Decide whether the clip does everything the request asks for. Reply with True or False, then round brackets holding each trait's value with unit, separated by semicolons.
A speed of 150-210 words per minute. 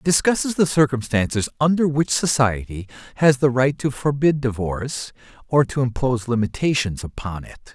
False (140 wpm)